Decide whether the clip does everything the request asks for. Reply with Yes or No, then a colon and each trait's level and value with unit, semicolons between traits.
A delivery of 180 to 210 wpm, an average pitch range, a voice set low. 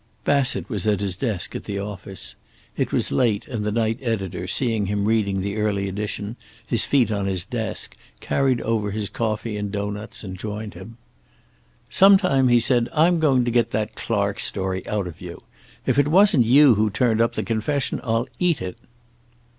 Yes: average, 185 wpm; average, 3.4 semitones; low, 110 Hz